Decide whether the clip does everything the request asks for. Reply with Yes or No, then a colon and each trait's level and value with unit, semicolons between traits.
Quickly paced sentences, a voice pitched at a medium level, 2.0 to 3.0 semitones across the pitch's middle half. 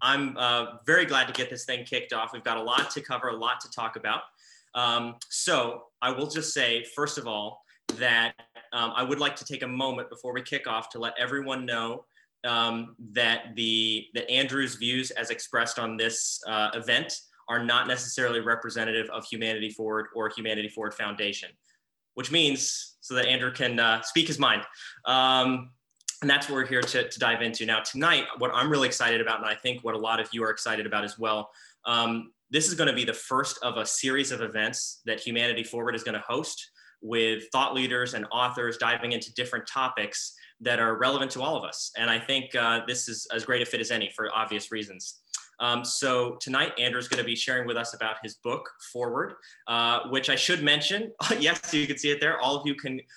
No: fast, 215 wpm; low, 120 Hz; narrow, 2.4 semitones